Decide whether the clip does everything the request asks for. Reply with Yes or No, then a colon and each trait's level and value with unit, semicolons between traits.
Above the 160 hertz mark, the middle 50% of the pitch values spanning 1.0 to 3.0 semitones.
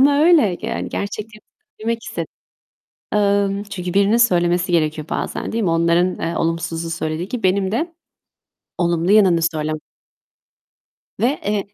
No: high, 190 Hz; average, 4.1 semitones